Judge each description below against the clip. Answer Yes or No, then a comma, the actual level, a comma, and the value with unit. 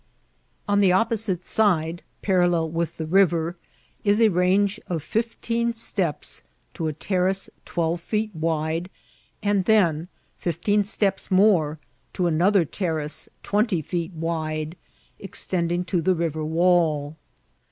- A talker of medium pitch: Yes, medium, 175 Hz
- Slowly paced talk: Yes, slow, 120 wpm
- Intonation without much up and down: No, average, 3.7 semitones